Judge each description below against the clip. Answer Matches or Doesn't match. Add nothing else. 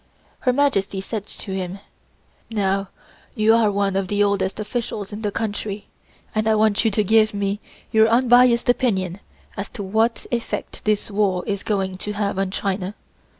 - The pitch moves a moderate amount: Doesn't match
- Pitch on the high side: Matches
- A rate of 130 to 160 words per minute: Doesn't match